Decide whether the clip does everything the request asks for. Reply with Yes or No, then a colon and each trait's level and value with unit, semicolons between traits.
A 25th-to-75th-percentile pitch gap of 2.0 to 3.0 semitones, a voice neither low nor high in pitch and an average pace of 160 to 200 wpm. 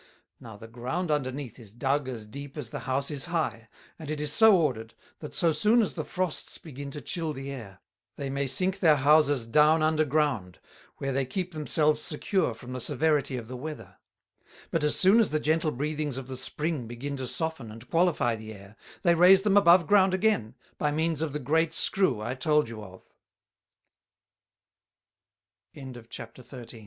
No: average, 4.2 semitones; medium, 145 Hz; average, 180 wpm